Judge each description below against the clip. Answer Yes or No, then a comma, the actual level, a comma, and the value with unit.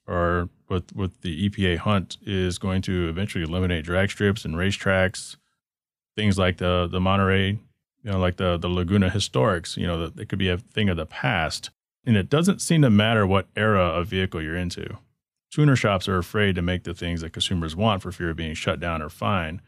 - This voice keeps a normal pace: No, fast, 210 wpm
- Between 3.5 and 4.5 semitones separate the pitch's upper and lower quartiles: No, average, 2.7 semitones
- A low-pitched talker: Yes, very low, 95 Hz